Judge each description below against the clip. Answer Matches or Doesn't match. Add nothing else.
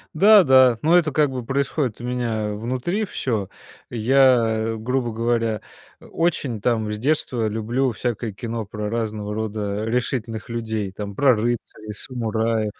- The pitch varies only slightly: Doesn't match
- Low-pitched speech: Matches